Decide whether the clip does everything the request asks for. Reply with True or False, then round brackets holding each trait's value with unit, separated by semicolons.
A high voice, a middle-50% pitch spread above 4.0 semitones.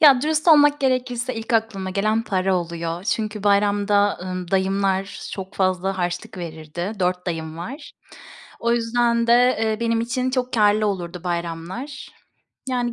True (205 Hz; 4.6 semitones)